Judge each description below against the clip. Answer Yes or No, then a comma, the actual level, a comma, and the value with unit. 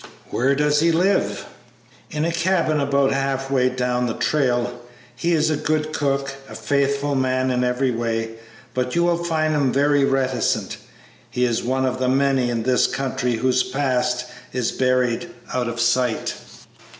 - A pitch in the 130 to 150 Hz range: Yes, low, 135 Hz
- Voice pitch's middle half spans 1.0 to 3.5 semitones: Yes, narrow, 2.6 semitones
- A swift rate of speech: No, average, 160 wpm